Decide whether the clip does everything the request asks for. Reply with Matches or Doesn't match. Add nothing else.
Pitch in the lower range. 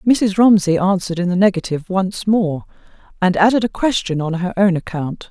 Doesn't match